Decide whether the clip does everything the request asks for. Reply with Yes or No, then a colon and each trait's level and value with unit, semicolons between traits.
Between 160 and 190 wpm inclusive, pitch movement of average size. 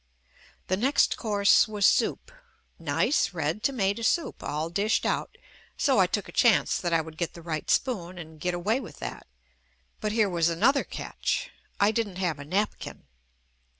Yes: average, 180 wpm; average, 4.7 semitones